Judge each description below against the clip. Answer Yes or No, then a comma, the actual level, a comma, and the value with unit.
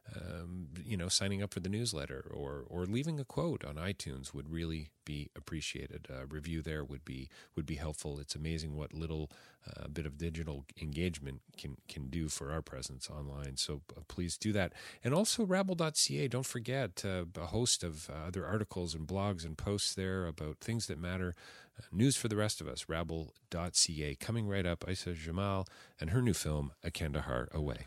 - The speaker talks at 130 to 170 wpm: No, average, 190 wpm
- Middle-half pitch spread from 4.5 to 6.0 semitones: Yes, average, 4.8 semitones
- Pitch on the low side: Yes, very low, 85 Hz